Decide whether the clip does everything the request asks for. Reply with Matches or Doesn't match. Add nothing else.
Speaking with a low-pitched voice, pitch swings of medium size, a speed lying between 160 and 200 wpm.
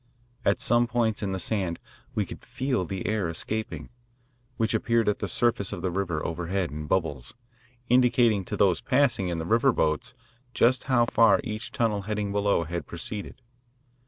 Matches